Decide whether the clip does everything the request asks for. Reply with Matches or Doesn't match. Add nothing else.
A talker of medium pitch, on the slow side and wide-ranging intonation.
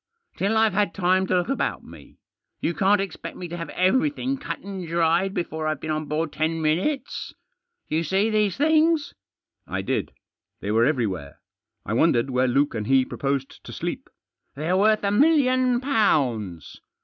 Doesn't match